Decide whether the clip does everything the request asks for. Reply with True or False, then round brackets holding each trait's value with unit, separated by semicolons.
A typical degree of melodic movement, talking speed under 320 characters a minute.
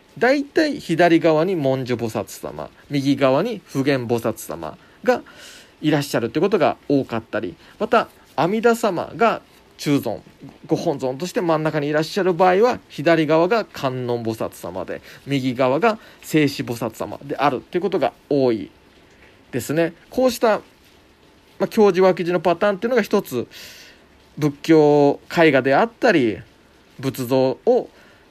False (6.7 semitones; 285 characters per minute)